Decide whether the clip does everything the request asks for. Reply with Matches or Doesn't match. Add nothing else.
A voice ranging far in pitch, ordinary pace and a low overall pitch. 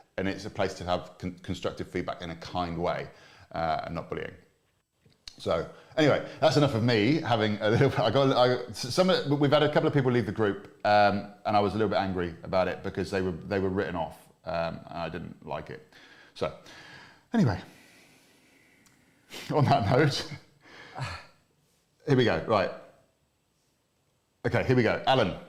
Matches